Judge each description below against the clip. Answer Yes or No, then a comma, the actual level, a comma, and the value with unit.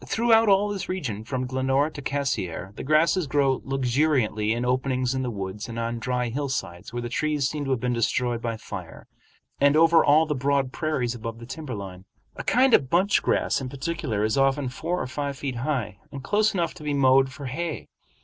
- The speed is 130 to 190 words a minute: No, fast, 205 wpm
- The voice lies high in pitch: No, low, 135 Hz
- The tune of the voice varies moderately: Yes, average, 4.1 semitones